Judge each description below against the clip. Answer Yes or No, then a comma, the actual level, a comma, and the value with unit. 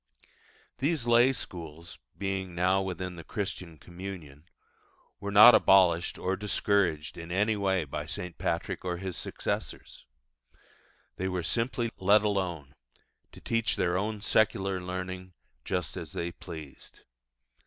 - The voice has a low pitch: Yes, very low, 95 Hz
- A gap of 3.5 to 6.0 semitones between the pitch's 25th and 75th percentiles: No, average, 2.7 semitones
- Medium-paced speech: No, slow, 130 wpm